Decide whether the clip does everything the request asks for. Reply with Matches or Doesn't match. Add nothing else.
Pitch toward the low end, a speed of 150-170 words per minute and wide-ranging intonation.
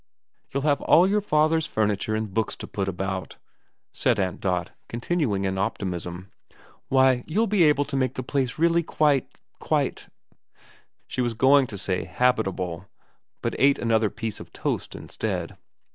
Matches